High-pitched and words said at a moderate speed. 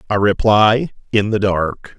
No: low, 105 Hz; average, 150 wpm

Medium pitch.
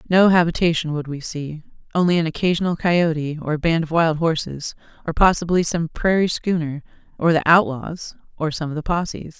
Yes: medium, 165 Hz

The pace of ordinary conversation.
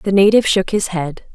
No: fast, 225 wpm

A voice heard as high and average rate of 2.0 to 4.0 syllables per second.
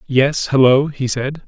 No: low, 135 Hz; 3.9 syllables/s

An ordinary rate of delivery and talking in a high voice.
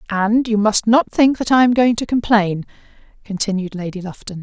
Yes: average, 190 wpm; high, 215 Hz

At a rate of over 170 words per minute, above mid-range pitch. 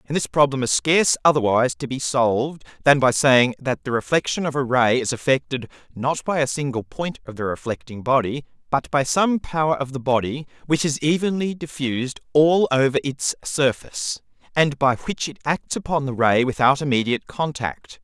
No: average, 185 wpm; medium, 140 Hz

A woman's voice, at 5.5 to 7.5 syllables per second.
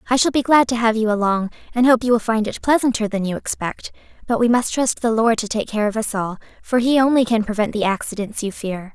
Yes: female; 5.9 syllables/s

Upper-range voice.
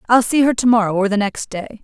Yes: high, 220 Hz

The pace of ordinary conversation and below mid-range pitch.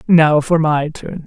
No: average, 190 wpm; medium, 155 Hz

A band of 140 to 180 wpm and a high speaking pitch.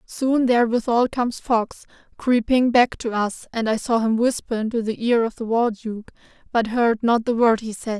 No: fast, 205 wpm; high, 230 Hz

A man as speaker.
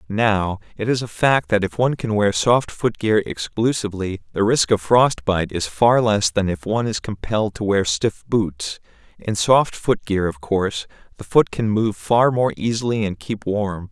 Yes: male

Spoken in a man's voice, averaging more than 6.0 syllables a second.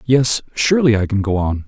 No: male; 5.5 syllables/s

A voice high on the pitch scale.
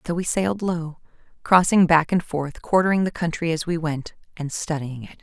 No: medium, 165 Hz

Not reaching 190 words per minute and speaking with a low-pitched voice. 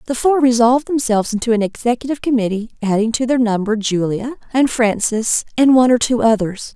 No: average, 180 wpm; high, 235 Hz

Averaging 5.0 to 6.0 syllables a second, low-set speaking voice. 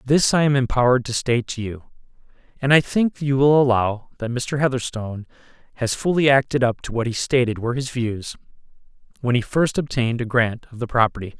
Yes: 5.8 syllables/s; low, 125 Hz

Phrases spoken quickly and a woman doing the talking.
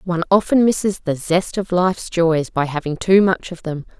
Yes: fast, 210 wpm; female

